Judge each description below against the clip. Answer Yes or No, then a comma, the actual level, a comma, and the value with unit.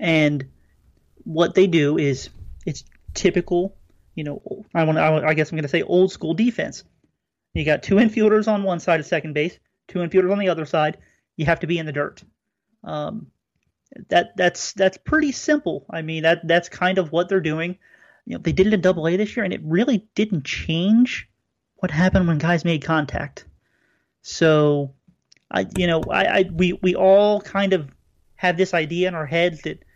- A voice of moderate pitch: Yes, medium, 175 Hz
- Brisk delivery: No, average, 195 wpm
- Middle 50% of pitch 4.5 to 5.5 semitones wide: No, average, 3.1 semitones